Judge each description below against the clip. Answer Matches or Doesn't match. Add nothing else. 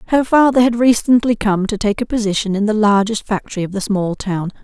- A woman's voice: Matches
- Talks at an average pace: Doesn't match